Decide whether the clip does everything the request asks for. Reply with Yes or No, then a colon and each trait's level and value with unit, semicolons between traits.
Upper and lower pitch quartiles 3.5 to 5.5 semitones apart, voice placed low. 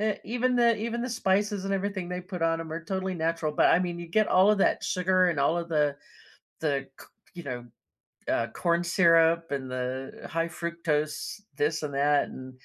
No: average, 3.8 semitones; medium, 170 Hz